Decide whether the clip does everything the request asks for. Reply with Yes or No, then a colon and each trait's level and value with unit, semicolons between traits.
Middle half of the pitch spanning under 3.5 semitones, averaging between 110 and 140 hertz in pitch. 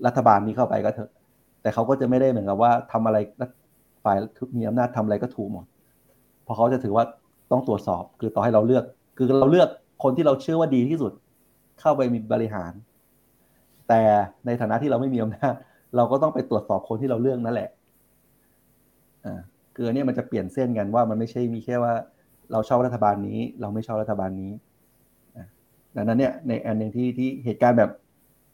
Yes: average, 2.8 semitones; low, 115 Hz